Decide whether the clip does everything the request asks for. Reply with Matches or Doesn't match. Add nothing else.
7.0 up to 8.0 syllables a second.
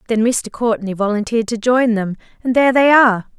Doesn't match